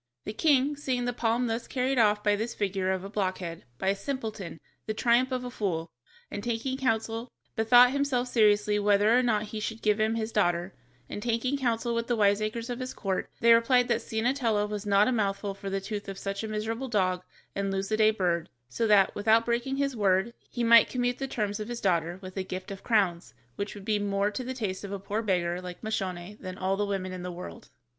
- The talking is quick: Yes, fast, 220 wpm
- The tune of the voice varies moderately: Yes, average, 3.3 semitones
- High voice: Yes, high, 210 Hz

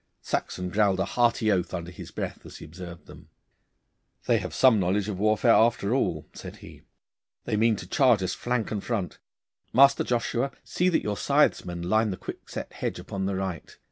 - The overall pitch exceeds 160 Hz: No, low, 105 Hz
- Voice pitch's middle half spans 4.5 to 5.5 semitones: No, average, 4.1 semitones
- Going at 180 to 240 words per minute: Yes, average, 185 wpm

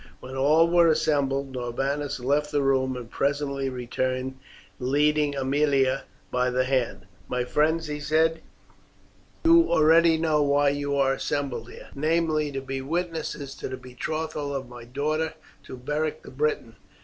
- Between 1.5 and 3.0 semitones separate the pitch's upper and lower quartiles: Yes, average, 2.7 semitones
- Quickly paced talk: No, average, 150 wpm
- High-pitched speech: No, medium, 140 Hz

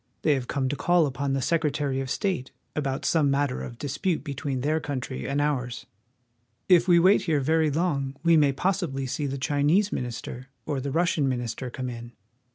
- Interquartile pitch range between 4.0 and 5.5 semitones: No, average, 3.3 semitones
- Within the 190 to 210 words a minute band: Yes, average, 200 wpm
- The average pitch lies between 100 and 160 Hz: Yes, medium, 140 Hz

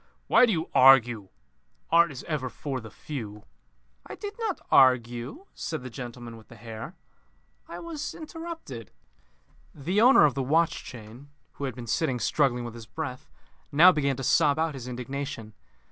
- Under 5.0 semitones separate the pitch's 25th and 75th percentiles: No, average, 5.3 semitones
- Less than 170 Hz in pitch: Yes, low, 135 Hz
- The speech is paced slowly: No, average, 165 wpm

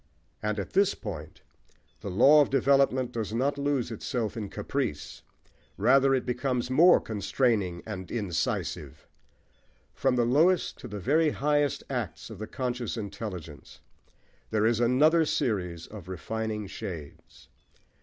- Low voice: Yes, low, 120 Hz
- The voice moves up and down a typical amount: Yes, average, 4.9 semitones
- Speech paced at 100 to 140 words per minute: Yes, slow, 135 wpm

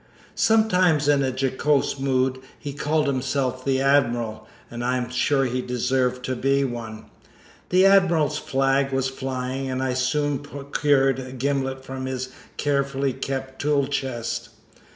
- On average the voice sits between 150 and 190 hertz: No, low, 135 Hz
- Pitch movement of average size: No, narrow, 1.7 semitones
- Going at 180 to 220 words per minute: No, average, 145 wpm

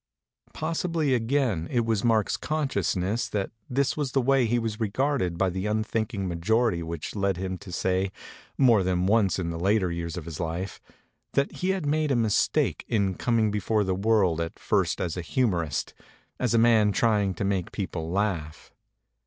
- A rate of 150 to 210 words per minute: Yes, average, 180 wpm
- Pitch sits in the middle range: No, low, 105 Hz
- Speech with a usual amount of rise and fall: Yes, average, 4.5 semitones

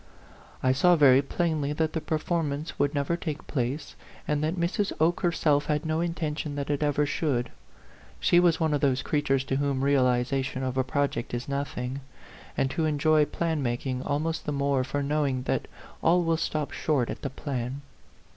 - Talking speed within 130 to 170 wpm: No, average, 185 wpm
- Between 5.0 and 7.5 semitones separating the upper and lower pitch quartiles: No, average, 2.8 semitones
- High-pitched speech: No, medium, 145 Hz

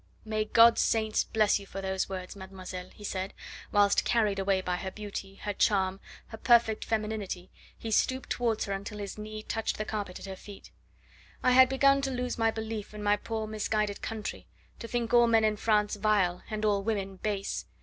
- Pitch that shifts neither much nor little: No, narrow, 2.2 semitones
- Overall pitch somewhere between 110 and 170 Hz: No, high, 210 Hz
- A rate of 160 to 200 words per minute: Yes, average, 195 wpm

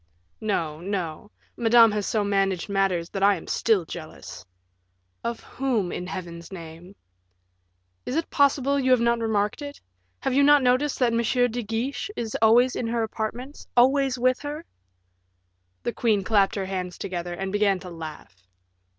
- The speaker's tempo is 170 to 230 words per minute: No, average, 160 wpm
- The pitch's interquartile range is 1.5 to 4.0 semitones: No, average, 4.9 semitones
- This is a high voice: Yes, high, 220 Hz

